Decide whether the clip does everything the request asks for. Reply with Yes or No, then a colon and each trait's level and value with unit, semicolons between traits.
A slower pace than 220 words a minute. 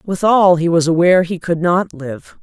Yes: average, 200 wpm